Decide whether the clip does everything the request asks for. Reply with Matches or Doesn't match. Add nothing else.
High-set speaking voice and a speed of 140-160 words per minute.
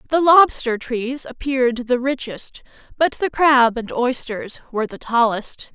Matches